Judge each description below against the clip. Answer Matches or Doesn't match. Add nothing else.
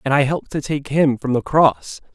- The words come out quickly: Matches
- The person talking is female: Doesn't match